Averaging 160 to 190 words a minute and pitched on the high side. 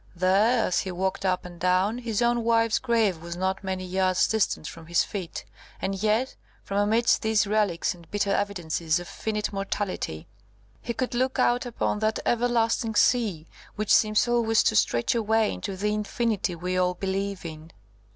Yes: average, 170 wpm; high, 200 Hz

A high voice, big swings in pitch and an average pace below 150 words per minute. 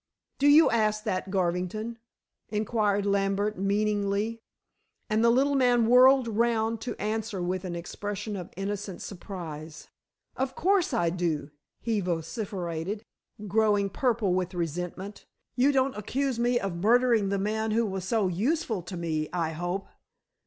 No: high, 205 Hz; average, 4.0 semitones; average, 140 wpm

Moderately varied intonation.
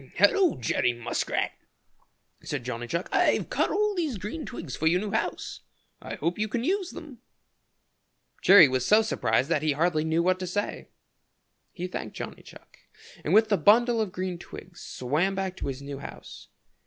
No: wide, 6.2 semitones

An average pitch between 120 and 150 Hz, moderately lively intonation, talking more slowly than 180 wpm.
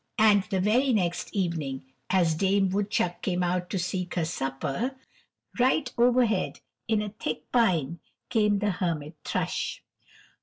No: high, 190 Hz; average, 3.8 semitones; average, 140 wpm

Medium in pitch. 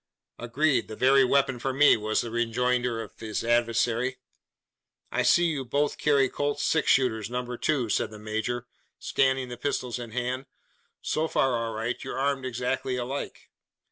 No: low, 125 Hz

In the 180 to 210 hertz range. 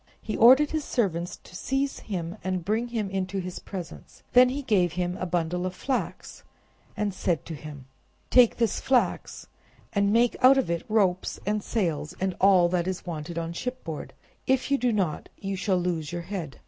Yes: high, 190 Hz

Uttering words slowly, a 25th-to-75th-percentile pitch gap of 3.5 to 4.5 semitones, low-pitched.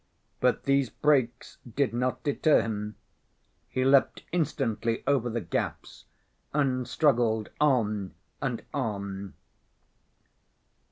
Yes: slow, 100 wpm; average, 3.9 semitones; low, 125 Hz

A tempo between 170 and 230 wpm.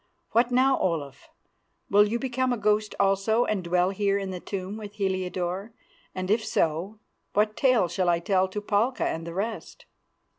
Yes: average, 175 wpm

